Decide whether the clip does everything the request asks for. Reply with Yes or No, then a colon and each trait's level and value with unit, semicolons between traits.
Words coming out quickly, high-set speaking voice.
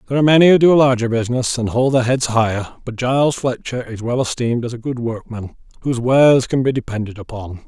No: fast, 225 wpm; low, 125 Hz